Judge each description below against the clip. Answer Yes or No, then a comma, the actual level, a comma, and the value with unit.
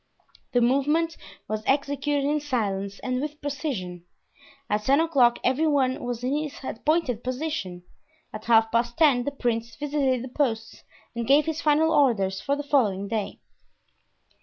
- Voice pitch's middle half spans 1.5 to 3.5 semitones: No, average, 4.3 semitones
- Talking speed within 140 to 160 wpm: Yes, average, 155 wpm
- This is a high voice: Yes, very high, 260 Hz